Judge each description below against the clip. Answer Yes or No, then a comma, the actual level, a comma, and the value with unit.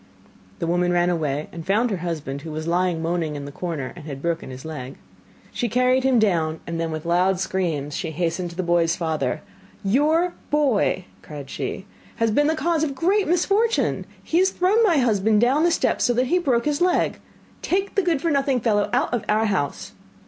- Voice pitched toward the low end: No, high, 190 Hz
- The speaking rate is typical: No, fast, 210 wpm